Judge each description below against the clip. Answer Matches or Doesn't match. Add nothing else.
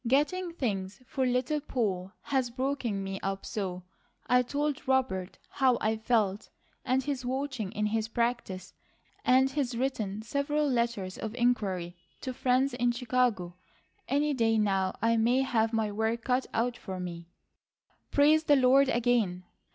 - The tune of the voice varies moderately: Matches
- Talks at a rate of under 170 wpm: Matches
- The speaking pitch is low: Doesn't match